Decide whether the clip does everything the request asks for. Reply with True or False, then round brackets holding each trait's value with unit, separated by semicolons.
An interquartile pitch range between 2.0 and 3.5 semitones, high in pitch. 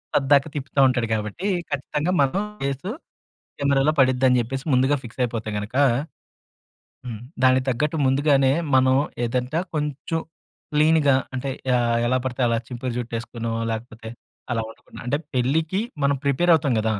False (3.0 semitones; 130 Hz)